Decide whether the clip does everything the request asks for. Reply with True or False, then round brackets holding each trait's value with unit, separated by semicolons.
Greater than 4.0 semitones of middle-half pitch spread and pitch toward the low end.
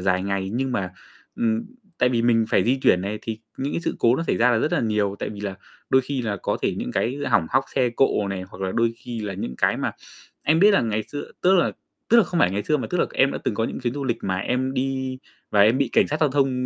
True (4.6 semitones; 120 Hz)